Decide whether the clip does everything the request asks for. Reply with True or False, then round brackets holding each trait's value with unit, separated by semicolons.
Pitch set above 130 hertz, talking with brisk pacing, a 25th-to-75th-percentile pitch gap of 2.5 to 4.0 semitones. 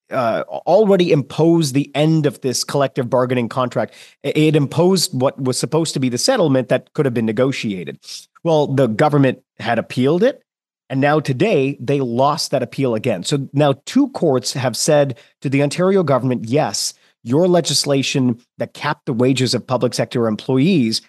False (140 Hz; 170 wpm; 3.1 semitones)